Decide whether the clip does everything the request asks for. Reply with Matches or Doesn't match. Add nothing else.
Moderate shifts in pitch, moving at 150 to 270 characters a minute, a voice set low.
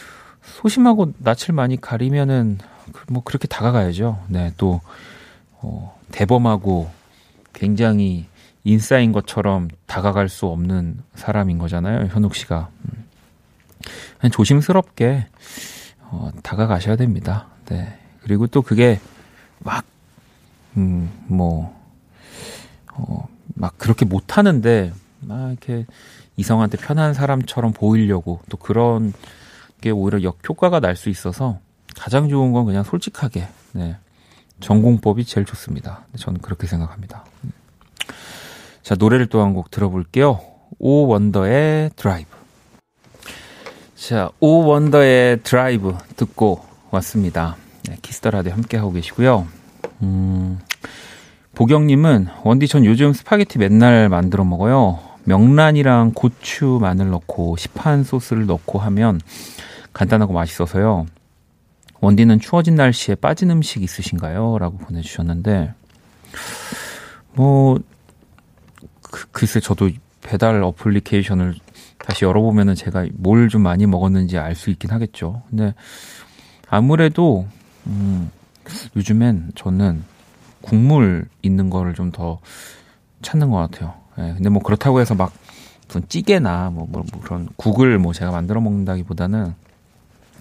Matches